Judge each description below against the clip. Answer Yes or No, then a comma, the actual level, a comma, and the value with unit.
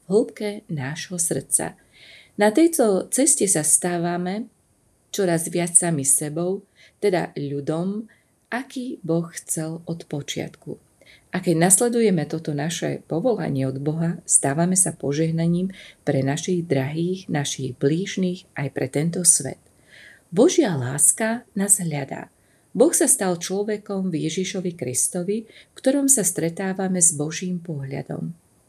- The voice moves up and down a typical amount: Yes, average, 4.4 semitones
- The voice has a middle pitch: Yes, medium, 175 Hz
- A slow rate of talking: No, average, 120 wpm